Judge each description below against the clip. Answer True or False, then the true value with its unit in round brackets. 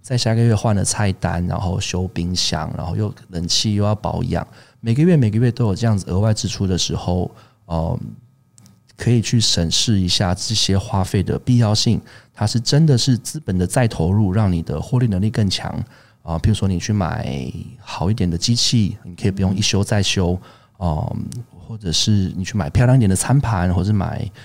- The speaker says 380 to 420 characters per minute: False (285 characters per minute)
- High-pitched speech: False (105 Hz)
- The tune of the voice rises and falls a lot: False (4.1 semitones)